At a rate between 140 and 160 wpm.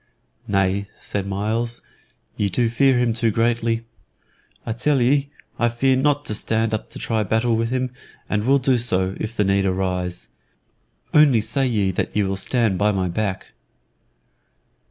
No: average, 170 wpm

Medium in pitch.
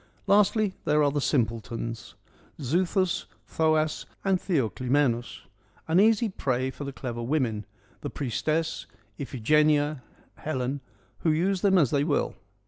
Yes: medium, 145 Hz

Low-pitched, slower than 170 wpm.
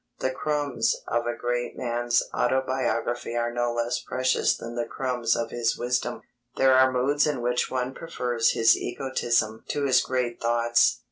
Yes: low, 120 Hz; average, 160 wpm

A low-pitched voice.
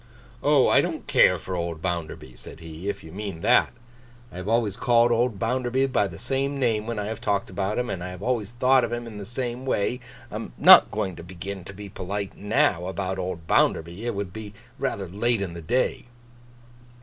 Yes: low, 100 Hz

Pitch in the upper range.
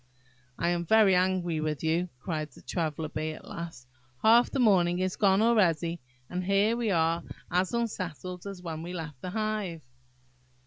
No: medium, 180 Hz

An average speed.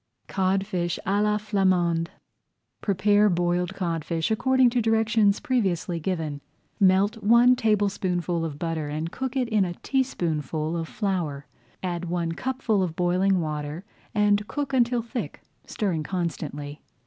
No: slow, 130 wpm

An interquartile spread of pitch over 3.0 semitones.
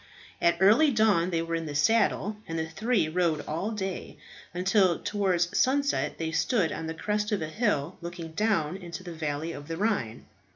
Yes: average, 4.4 semitones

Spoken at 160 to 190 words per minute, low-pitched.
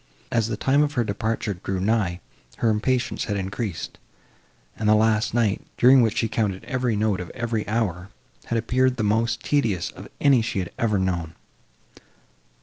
Yes: average, 170 wpm; low, 110 Hz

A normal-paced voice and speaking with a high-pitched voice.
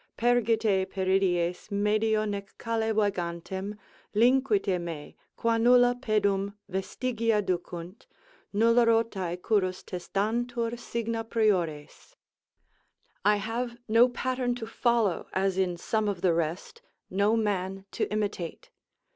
No: slow, 110 wpm; high, 210 Hz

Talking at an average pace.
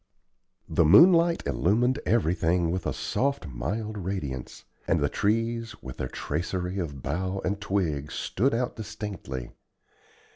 No: slow, 125 wpm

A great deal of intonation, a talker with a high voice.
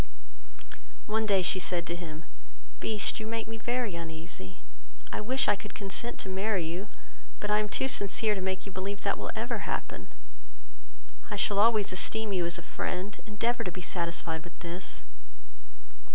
No: average, 3.5 semitones; high, 195 Hz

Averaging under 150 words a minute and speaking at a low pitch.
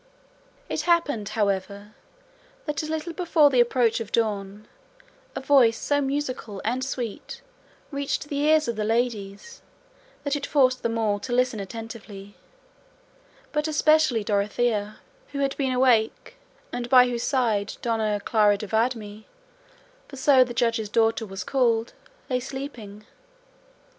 No: average, 140 wpm; high, 235 Hz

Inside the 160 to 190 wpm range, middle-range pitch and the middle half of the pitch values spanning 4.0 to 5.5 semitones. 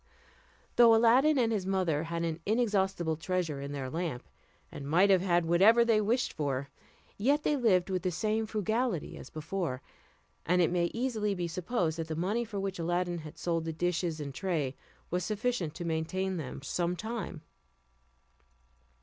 Yes: average, 170 wpm; medium, 180 Hz; average, 4.6 semitones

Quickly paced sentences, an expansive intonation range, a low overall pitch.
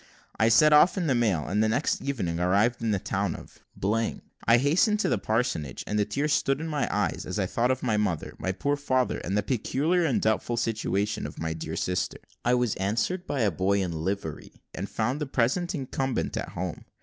Yes: fast, 215 wpm; wide, 5.9 semitones; low, 115 Hz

